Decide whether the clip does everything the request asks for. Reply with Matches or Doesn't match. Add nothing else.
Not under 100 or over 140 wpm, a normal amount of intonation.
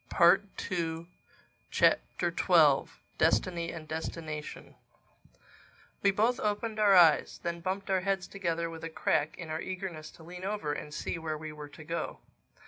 Doesn't match